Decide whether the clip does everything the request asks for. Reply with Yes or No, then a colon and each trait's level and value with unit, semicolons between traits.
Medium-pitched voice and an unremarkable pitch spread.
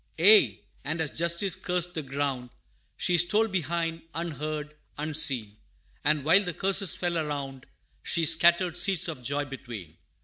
Yes: medium, 160 Hz; average, 3.6 semitones